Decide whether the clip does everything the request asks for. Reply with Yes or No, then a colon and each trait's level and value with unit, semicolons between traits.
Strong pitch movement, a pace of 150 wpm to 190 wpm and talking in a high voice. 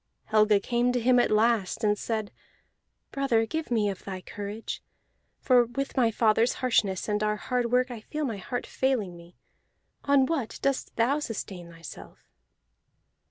No: average, 3.4 semitones; average, 160 wpm; high, 230 Hz